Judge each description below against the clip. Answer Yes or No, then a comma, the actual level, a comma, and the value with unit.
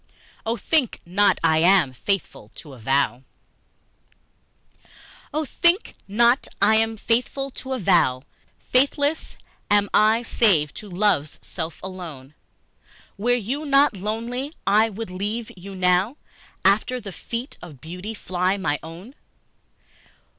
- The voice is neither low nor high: No, high, 205 Hz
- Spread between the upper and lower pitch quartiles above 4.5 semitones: Yes, average, 5.1 semitones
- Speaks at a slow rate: Yes, slow, 130 wpm